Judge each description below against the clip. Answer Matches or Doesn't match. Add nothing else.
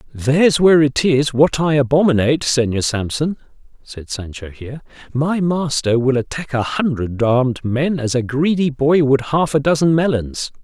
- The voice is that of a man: Matches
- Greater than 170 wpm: Doesn't match